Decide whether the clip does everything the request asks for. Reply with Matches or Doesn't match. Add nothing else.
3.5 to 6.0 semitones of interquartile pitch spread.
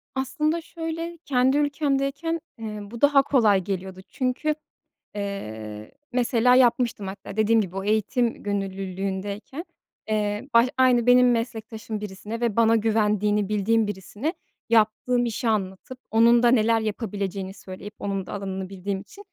Matches